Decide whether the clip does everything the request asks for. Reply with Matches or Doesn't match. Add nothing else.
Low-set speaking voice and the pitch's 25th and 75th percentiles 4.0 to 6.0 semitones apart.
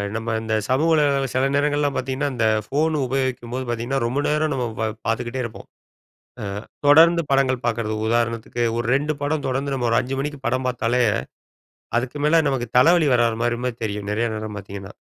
Doesn't match